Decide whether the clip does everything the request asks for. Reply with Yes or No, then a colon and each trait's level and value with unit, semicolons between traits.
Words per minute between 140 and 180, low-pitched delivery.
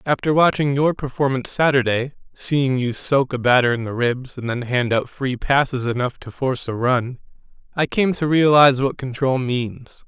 Yes: average, 175 wpm; low, 130 Hz